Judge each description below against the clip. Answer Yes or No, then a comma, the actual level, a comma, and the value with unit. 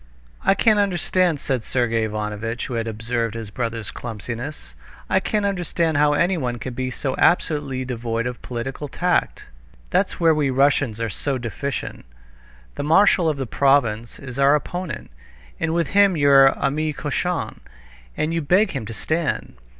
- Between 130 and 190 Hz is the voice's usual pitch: Yes, low, 135 Hz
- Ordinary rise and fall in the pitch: No, wide, 5.7 semitones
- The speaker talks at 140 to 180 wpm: Yes, average, 160 wpm